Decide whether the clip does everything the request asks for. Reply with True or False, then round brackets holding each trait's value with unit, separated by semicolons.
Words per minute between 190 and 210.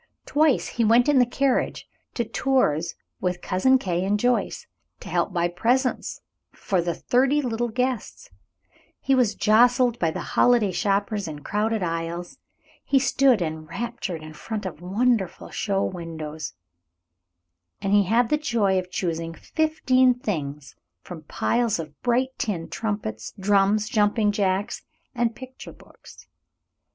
False (140 wpm)